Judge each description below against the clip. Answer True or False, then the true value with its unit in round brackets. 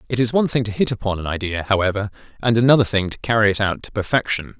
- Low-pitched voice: True (110 Hz)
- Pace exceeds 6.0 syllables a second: True (7.1 syllables/s)